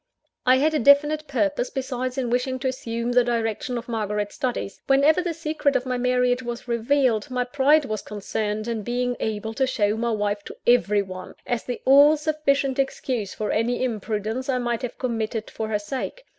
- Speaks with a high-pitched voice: Yes, high, 245 Hz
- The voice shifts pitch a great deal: No, average, 3.3 semitones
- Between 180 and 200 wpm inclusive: Yes, average, 190 wpm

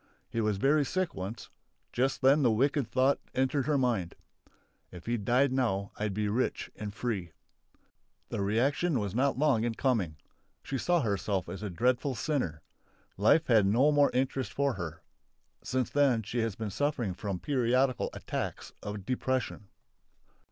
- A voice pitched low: Yes, low, 120 Hz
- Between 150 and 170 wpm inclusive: Yes, average, 160 wpm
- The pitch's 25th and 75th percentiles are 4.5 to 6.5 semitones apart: Yes, average, 4.8 semitones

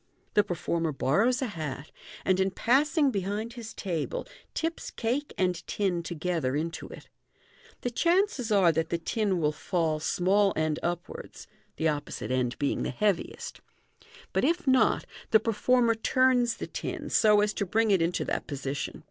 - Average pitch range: No, wide, 6.3 semitones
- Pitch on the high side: Yes, high, 195 Hz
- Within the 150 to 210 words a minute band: Yes, average, 165 wpm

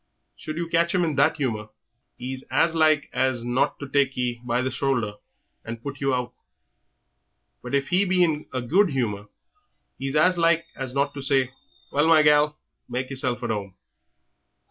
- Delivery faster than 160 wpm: Yes, average, 180 wpm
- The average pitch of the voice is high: No, medium, 140 Hz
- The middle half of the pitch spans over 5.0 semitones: No, average, 3.8 semitones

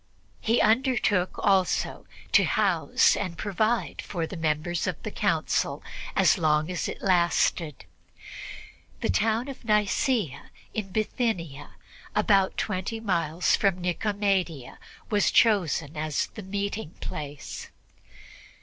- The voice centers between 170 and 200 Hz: Yes, high, 190 Hz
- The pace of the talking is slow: Yes, slow, 115 wpm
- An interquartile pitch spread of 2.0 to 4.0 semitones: No, average, 4.7 semitones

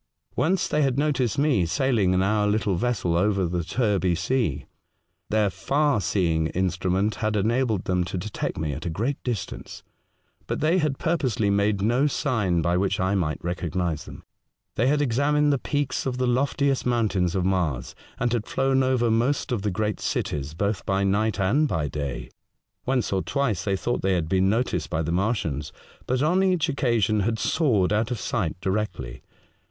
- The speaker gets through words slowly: No, average, 180 wpm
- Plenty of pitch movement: Yes, wide, 6.0 semitones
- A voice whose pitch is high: No, low, 105 Hz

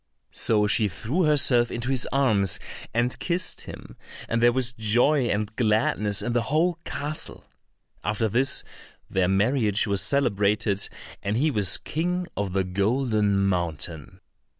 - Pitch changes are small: No, average, 4.7 semitones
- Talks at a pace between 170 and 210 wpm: No, average, 140 wpm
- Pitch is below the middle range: Yes, low, 110 Hz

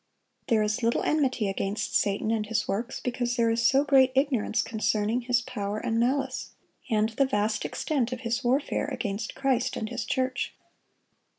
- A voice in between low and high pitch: No, high, 235 Hz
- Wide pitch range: No, average, 3.3 semitones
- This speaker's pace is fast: No, average, 170 wpm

